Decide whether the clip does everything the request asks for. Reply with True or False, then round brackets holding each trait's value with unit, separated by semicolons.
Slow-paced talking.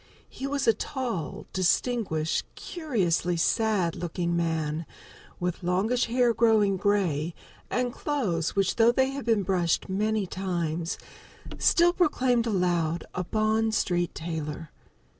True (120 wpm)